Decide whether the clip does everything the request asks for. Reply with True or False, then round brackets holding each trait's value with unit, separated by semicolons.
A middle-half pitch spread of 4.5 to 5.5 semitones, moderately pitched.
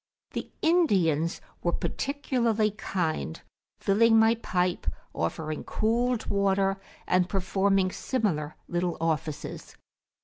False (4.9 semitones; 195 Hz)